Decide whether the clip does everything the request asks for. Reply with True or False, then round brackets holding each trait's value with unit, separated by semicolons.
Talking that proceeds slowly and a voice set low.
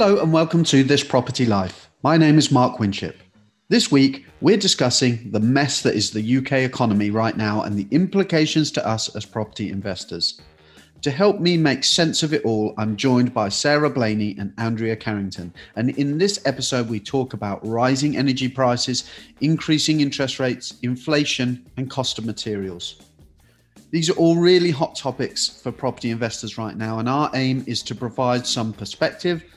False (175 wpm; 125 Hz)